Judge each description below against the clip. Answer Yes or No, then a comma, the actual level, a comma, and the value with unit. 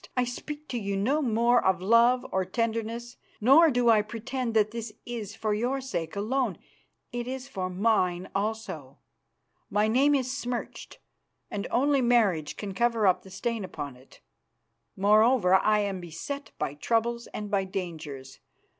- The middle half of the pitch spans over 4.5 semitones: No, average, 4.2 semitones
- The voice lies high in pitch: Yes, high, 220 Hz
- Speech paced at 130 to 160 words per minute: Yes, average, 155 wpm